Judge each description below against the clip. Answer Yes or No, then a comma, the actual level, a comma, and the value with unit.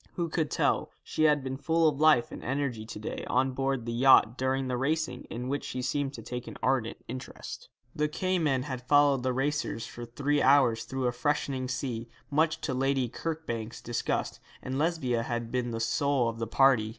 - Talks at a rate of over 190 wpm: Yes, average, 200 wpm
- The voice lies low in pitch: Yes, low, 130 Hz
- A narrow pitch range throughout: No, average, 3.0 semitones